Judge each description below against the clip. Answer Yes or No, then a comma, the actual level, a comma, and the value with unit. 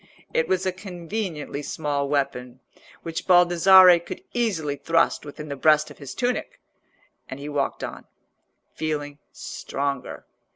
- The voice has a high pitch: No, medium, 155 Hz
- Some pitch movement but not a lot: Yes, average, 3.9 semitones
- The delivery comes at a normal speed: No, slow, 130 wpm